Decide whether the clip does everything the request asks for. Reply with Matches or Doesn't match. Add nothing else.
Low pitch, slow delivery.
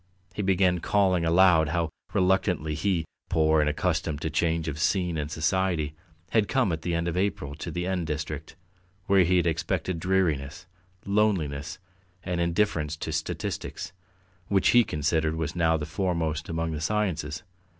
Doesn't match